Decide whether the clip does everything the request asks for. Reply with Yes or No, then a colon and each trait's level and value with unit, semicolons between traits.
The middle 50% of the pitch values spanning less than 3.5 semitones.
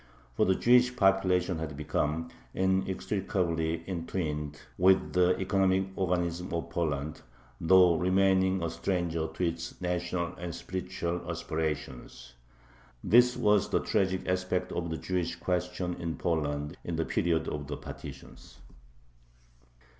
Yes: narrow, 2.5 semitones